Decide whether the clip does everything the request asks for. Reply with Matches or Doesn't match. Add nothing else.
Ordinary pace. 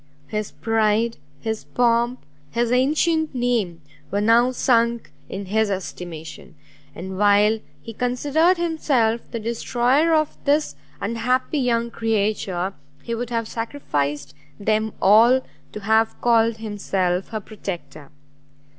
Doesn't match